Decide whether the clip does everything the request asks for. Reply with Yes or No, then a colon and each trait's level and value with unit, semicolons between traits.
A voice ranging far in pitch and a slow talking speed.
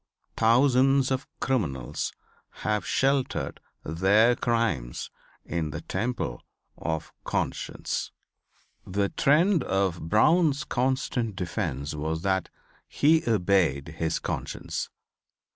Yes: wide, 8.1 semitones; slow, 95 wpm